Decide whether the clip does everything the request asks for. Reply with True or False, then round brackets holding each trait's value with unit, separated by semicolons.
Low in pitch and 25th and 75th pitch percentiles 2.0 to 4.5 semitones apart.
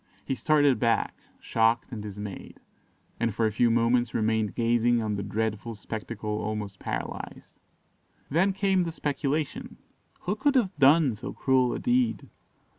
False (120 Hz; 5.4 semitones)